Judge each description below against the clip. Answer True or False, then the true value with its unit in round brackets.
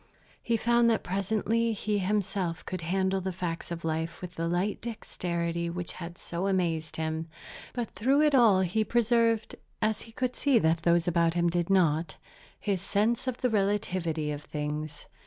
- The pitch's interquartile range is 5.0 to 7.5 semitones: False (4.6 semitones)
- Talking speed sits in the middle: True (175 wpm)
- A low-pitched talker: False (185 Hz)